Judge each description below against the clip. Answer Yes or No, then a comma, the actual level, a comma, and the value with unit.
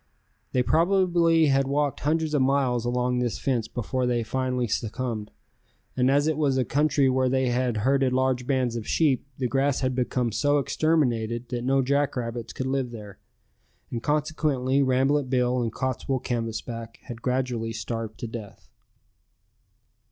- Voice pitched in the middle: No, low, 130 Hz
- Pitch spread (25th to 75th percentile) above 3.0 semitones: No, narrow, 2.5 semitones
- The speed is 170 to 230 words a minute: No, average, 155 wpm